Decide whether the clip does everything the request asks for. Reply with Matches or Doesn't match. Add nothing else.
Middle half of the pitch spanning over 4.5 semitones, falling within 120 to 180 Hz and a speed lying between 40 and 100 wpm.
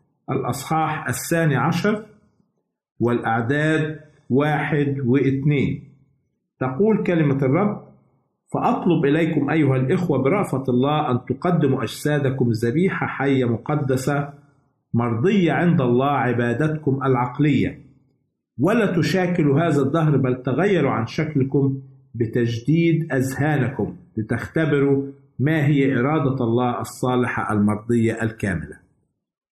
Doesn't match